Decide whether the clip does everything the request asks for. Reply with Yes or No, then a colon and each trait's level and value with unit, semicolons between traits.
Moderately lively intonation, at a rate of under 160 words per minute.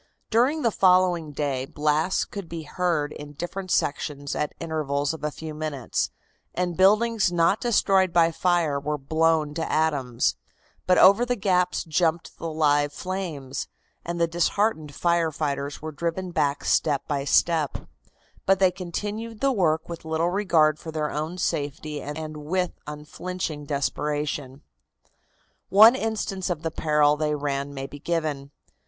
Yes: average, 3.6 semitones; average, 150 wpm